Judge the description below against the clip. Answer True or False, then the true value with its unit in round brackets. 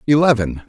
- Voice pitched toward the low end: True (120 Hz)